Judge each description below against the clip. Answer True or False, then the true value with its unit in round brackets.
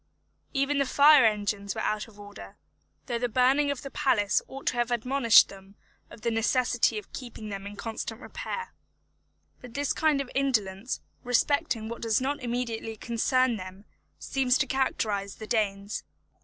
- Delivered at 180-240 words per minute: False (165 wpm)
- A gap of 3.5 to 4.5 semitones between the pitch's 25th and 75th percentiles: True (4.0 semitones)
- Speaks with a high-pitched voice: True (235 Hz)